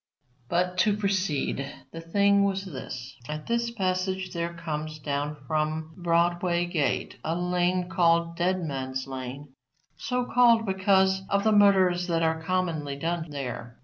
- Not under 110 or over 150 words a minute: Yes, average, 145 wpm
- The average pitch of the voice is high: No, medium, 175 Hz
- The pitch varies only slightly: No, average, 3.7 semitones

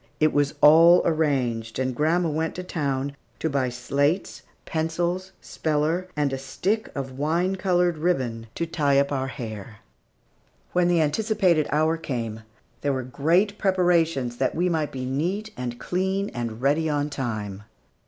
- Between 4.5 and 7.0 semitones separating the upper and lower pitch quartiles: Yes, average, 4.8 semitones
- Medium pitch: Yes, medium, 150 Hz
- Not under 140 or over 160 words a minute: Yes, average, 155 wpm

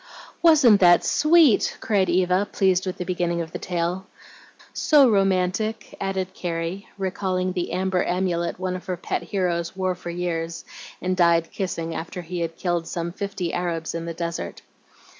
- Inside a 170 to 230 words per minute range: No, average, 160 wpm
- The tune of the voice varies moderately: No, narrow, 1.9 semitones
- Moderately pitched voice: Yes, medium, 180 Hz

